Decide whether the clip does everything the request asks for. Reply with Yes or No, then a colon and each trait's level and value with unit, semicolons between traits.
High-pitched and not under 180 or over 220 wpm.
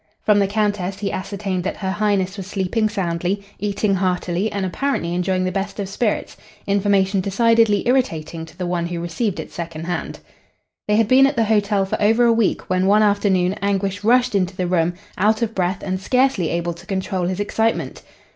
Yes: high, 195 Hz; average, 195 wpm